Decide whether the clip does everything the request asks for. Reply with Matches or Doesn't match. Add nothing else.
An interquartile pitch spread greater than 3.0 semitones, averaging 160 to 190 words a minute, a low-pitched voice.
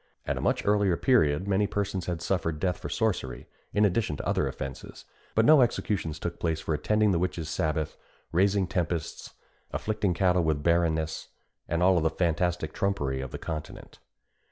Matches